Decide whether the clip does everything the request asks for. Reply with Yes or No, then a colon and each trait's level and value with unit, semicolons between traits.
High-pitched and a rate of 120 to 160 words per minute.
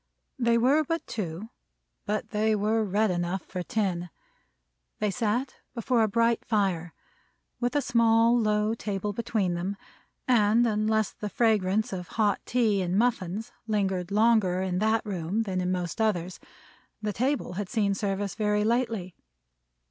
Yes: high, 210 Hz; average, 150 wpm